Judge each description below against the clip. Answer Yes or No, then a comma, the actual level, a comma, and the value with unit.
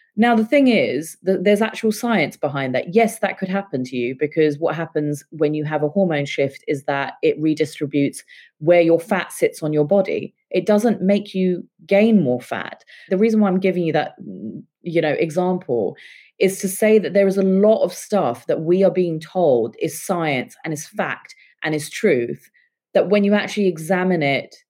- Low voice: No, medium, 180 Hz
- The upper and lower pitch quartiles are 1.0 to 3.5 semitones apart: No, average, 4.9 semitones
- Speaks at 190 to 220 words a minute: Yes, average, 200 wpm